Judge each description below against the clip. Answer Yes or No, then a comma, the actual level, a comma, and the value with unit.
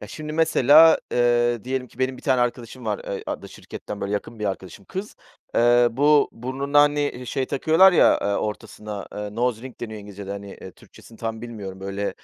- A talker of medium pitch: No, low, 120 Hz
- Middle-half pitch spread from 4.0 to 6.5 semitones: Yes, average, 4.3 semitones